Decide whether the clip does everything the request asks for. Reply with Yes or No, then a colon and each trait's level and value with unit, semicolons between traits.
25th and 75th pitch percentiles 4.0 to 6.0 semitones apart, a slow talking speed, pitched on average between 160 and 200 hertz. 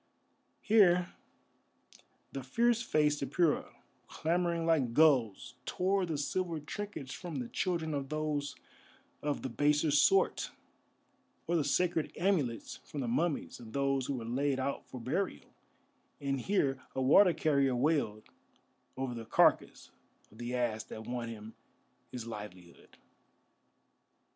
No: average, 5.2 semitones; slow, 130 wpm; medium, 140 Hz